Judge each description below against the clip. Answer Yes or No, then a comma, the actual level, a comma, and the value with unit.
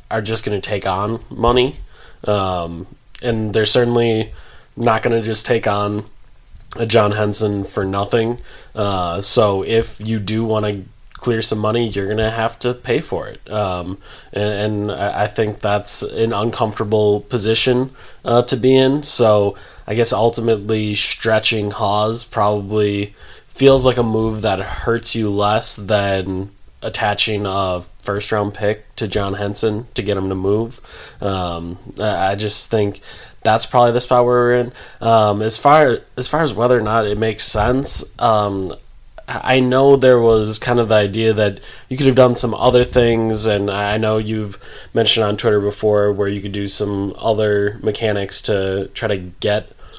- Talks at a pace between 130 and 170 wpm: Yes, average, 165 wpm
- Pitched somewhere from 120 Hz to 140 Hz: No, low, 110 Hz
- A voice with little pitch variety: Yes, narrow, 2.3 semitones